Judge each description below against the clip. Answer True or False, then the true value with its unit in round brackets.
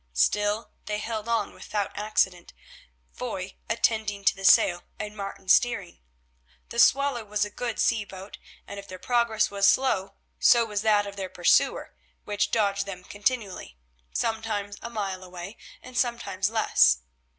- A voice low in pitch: False (205 Hz)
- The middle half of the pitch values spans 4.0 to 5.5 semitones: False (2.4 semitones)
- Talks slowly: False (150 wpm)